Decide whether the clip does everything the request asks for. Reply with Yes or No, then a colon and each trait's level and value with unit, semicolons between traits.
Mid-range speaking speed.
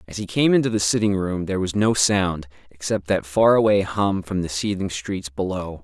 No: fast, 215 wpm